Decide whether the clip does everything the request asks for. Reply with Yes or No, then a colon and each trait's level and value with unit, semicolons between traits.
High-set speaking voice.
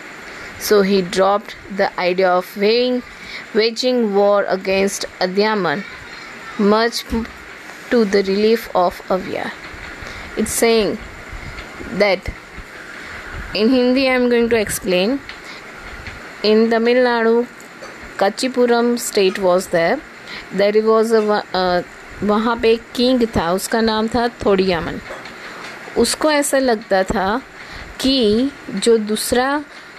Yes: high, 220 Hz